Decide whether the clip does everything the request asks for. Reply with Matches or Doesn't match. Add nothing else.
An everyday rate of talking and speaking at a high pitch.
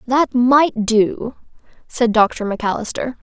Doesn't match